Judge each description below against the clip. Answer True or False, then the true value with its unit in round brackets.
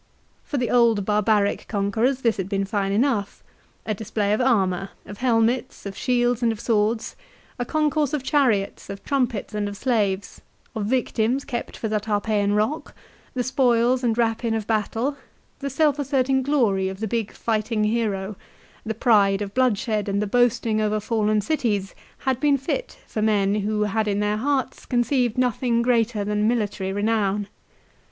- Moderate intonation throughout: True (3.2 semitones)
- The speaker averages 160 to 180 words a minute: True (165 wpm)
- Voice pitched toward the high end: True (220 Hz)